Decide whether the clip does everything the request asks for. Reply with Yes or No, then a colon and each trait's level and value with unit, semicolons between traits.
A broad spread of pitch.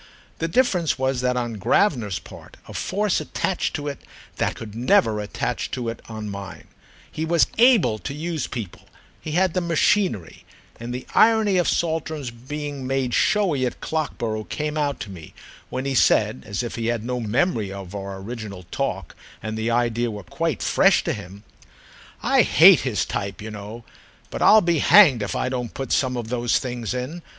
Yes: wide, 6.3 semitones